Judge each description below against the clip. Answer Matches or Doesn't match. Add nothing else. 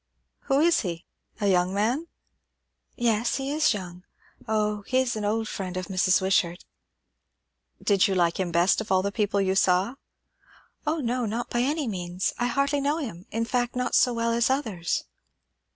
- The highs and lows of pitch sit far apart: Doesn't match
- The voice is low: Doesn't match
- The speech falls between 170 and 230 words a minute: Matches